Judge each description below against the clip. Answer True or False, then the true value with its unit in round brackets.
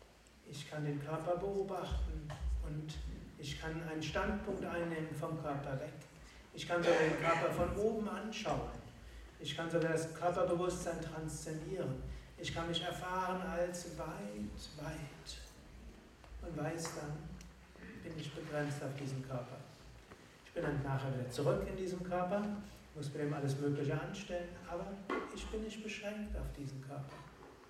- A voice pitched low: False (160 Hz)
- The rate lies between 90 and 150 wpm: True (145 wpm)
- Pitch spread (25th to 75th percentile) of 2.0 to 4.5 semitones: True (3.6 semitones)